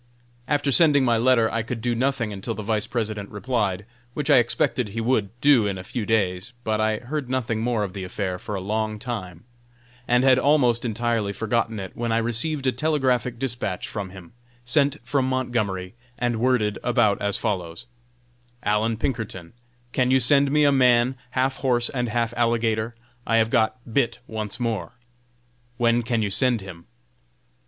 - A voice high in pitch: No, low, 115 Hz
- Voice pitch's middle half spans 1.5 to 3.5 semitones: Yes, average, 3.2 semitones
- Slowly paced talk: No, average, 175 wpm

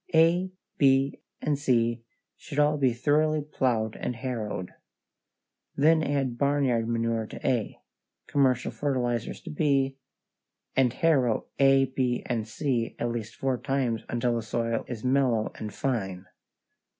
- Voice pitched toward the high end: No, low, 130 Hz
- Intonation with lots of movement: No, average, 3.3 semitones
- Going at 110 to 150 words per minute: Yes, slow, 135 wpm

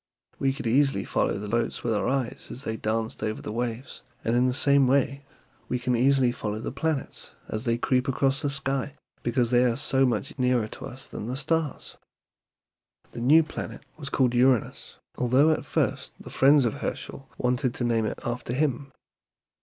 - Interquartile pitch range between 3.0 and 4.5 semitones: No, narrow, 2.5 semitones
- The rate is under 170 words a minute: No, average, 190 wpm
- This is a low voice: Yes, low, 125 Hz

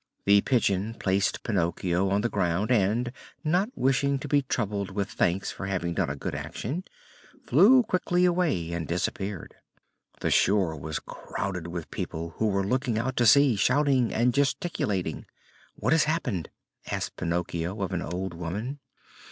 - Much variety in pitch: Yes, wide, 6.9 semitones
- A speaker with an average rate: Yes, average, 155 wpm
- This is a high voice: No, low, 100 Hz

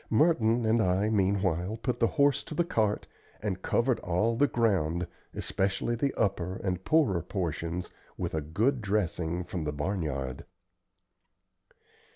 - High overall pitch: No, low, 100 Hz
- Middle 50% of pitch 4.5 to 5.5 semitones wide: Yes, average, 4.9 semitones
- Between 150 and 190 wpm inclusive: No, average, 140 wpm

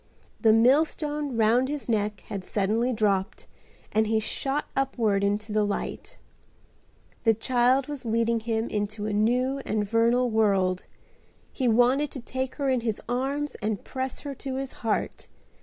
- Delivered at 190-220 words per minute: No, average, 155 wpm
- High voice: Yes, high, 230 Hz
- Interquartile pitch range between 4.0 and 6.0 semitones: No, average, 3.5 semitones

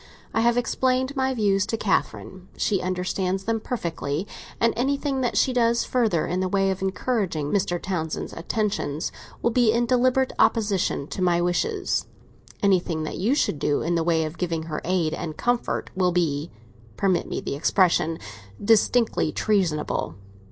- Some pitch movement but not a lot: No, wide, 5.9 semitones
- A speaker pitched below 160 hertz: No, high, 190 Hz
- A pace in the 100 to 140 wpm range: No, average, 155 wpm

